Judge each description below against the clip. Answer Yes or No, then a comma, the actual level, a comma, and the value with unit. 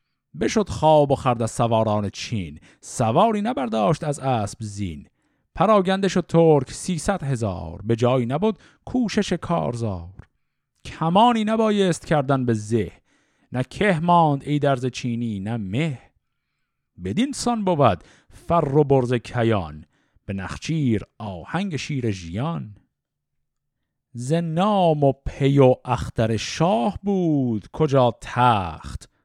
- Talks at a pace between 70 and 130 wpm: Yes, average, 115 wpm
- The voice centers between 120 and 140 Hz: Yes, low, 135 Hz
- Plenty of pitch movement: Yes, wide, 7.2 semitones